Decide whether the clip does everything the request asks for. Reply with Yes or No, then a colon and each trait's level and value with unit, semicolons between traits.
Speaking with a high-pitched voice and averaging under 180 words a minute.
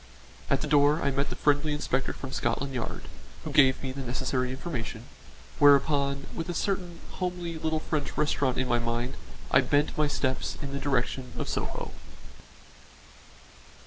No: medium, 140 Hz; average, 160 wpm